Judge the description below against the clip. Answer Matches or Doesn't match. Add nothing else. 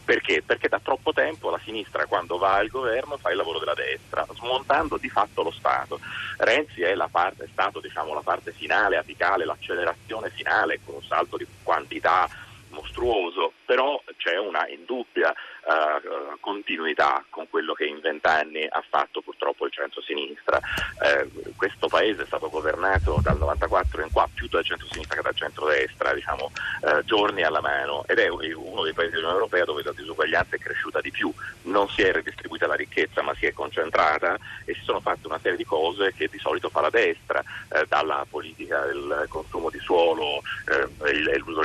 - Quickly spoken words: Matches